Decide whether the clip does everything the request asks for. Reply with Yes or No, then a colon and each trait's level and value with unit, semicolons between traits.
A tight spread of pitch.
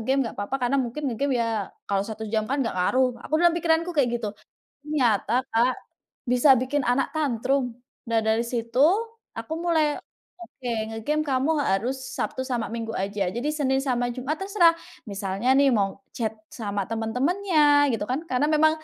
No: average, 4.6 semitones